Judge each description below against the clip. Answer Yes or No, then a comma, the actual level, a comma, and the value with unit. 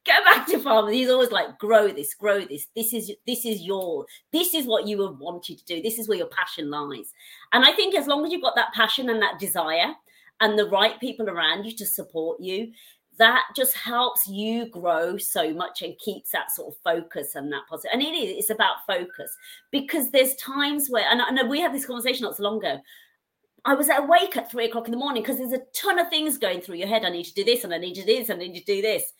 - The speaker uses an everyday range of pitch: No, wide, 6.0 semitones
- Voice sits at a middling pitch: No, high, 225 Hz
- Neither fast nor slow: No, fast, 255 wpm